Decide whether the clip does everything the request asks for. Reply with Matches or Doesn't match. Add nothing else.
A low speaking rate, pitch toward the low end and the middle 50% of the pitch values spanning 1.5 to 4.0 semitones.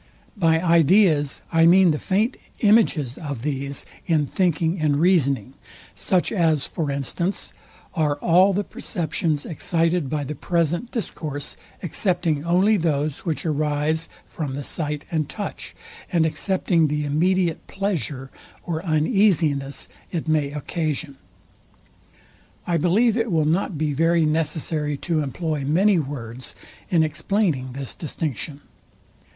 Doesn't match